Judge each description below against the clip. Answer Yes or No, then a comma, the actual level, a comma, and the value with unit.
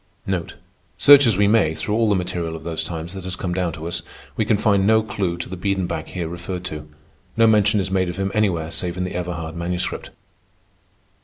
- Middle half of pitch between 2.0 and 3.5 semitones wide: Yes, average, 3.1 semitones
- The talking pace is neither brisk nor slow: No, fast, 215 wpm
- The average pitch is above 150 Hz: No, very low, 90 Hz